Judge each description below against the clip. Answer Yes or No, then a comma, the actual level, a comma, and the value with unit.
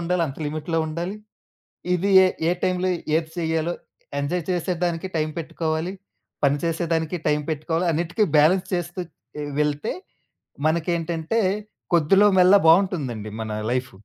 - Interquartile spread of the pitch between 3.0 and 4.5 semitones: No, narrow, 2.4 semitones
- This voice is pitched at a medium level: Yes, medium, 165 Hz